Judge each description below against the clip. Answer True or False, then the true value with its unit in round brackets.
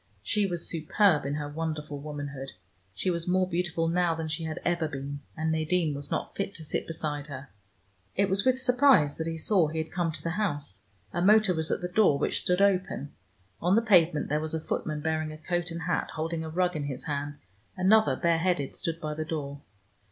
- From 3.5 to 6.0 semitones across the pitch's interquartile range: False (3.1 semitones)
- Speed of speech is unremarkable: False (215 wpm)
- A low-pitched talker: False (160 Hz)